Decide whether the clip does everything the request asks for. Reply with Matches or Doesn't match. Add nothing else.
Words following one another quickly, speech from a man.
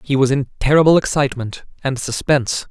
Doesn't match